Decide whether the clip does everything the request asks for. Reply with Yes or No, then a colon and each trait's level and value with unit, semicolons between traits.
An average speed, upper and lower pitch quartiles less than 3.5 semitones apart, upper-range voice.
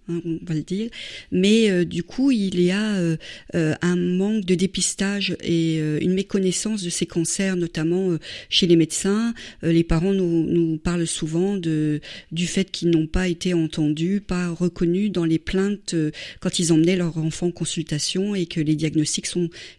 No: average, 190 wpm; narrow, 2.6 semitones; medium, 175 Hz